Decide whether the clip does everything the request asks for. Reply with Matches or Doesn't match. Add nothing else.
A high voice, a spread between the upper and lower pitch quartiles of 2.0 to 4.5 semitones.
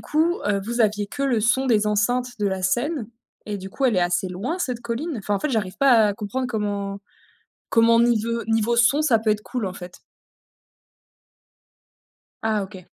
Matches